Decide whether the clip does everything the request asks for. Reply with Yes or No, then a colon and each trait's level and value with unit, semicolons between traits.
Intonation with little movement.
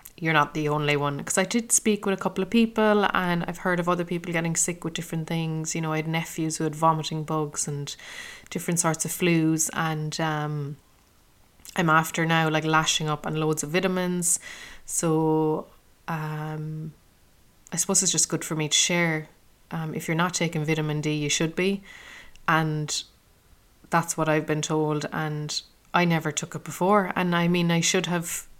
Yes: narrow, 2.2 semitones